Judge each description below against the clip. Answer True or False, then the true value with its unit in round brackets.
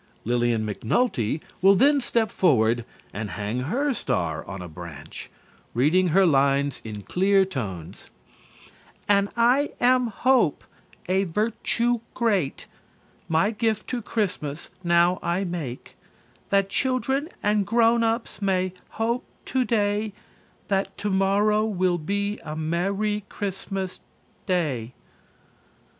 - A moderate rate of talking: False (115 wpm)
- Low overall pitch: False (195 Hz)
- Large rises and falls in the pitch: True (7.5 semitones)